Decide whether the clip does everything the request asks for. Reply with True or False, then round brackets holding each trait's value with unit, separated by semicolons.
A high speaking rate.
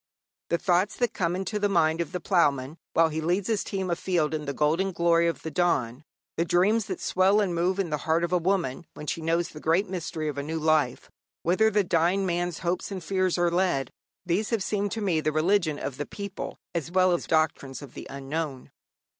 True (220 wpm)